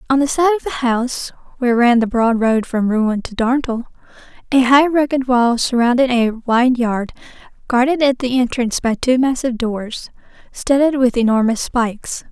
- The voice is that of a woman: Yes, female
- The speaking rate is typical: Yes, average, 170 wpm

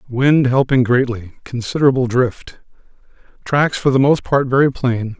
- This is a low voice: Yes, low, 125 Hz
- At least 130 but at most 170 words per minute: Yes, average, 140 wpm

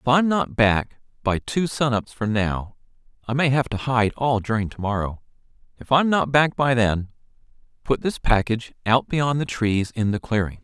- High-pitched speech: No, low, 120 Hz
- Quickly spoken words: No, average, 175 wpm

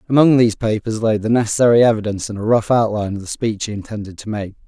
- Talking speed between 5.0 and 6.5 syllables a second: No, 7.1 syllables/s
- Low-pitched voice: Yes, low, 110 Hz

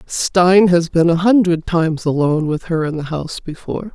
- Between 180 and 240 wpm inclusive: Yes, average, 200 wpm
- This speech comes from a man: No, female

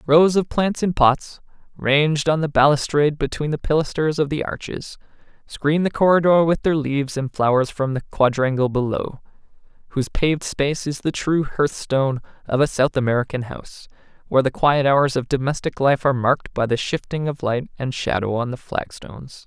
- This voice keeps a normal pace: Yes, average, 180 wpm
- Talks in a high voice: No, medium, 140 Hz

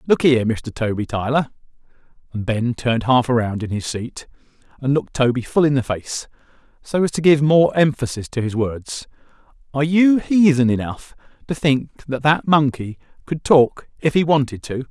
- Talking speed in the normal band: Yes, average, 170 wpm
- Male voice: Yes, male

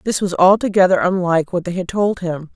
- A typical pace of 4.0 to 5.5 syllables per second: No, 5.8 syllables/s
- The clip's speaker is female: Yes, female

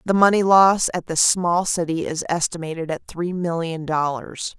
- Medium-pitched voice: Yes, medium, 170 Hz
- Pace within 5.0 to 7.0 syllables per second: No, 4.5 syllables/s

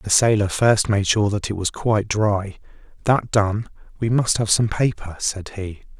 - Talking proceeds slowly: No, average, 190 wpm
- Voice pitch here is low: Yes, low, 105 Hz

